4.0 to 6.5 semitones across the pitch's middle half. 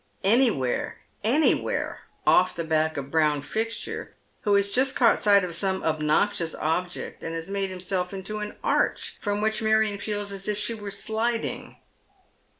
Yes: average, 4.4 semitones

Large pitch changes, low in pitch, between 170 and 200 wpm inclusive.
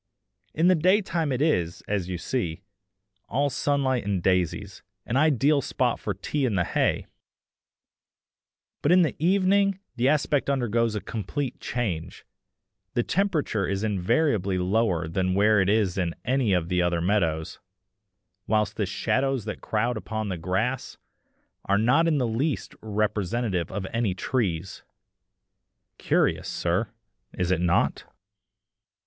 No: wide, 6.7 semitones; low, 110 Hz; average, 140 wpm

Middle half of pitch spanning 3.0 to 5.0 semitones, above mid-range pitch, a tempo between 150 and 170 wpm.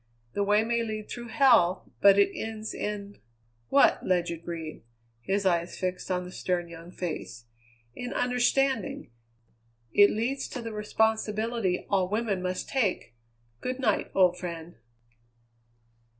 No: average, 3.9 semitones; high, 200 Hz; slow, 135 wpm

